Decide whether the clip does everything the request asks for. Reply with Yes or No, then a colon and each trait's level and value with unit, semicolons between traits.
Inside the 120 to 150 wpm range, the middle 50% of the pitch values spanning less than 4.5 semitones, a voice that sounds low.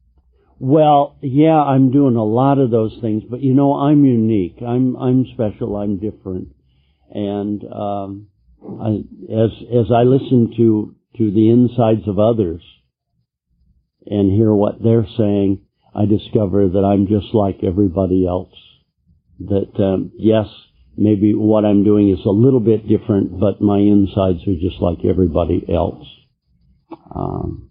Yes: average, 145 wpm; average, 3.2 semitones; low, 105 Hz